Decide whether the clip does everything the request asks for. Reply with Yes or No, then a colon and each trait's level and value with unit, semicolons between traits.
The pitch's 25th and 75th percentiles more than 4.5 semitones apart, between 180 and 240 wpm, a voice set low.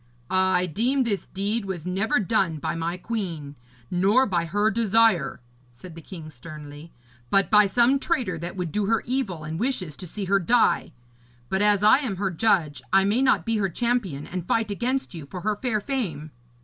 No: average, 5.0 semitones; average, 190 wpm; high, 195 Hz